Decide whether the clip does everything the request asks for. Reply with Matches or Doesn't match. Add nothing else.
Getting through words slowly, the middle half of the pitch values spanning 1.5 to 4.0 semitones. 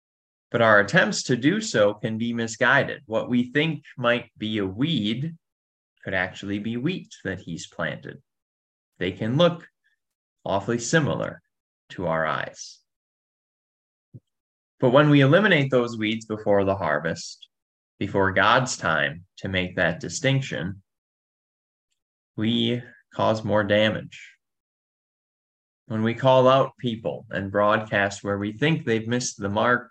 Doesn't match